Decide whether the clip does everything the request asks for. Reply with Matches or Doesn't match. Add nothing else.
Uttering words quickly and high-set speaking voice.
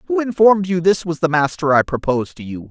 Doesn't match